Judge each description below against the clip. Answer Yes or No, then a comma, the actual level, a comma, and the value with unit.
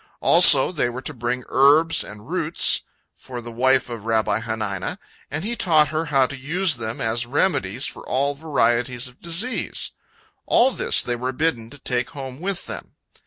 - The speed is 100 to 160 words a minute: No, average, 175 wpm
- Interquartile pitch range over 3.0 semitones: Yes, average, 4.9 semitones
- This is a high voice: No, low, 130 Hz